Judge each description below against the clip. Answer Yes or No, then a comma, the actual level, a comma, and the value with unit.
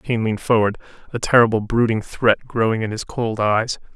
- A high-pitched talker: No, low, 110 Hz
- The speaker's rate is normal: Yes, average, 180 wpm